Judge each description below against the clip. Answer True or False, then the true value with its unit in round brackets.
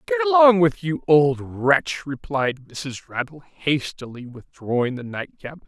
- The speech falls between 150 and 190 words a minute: False (135 wpm)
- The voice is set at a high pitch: False (150 Hz)